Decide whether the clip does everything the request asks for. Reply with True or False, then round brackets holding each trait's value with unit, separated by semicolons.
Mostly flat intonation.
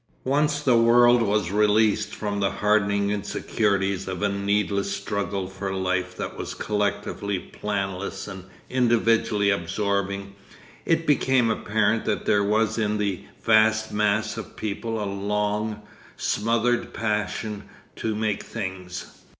True (1.9 semitones)